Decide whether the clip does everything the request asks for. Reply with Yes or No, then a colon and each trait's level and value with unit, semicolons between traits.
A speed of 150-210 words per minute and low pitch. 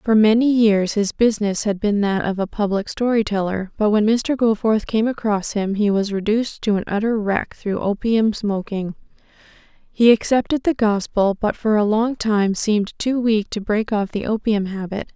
No: average, 190 wpm; high, 210 Hz